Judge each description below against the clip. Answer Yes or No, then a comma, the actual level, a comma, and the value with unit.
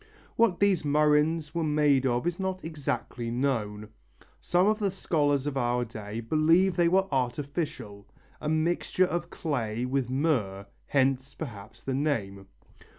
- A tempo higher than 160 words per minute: No, average, 145 wpm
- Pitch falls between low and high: Yes, medium, 145 Hz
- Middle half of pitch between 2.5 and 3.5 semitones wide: No, wide, 5.5 semitones